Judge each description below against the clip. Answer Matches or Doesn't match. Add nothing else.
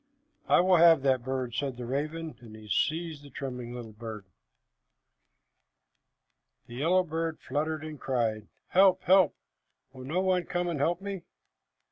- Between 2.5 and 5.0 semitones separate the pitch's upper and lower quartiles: Doesn't match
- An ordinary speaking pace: Matches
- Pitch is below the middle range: Doesn't match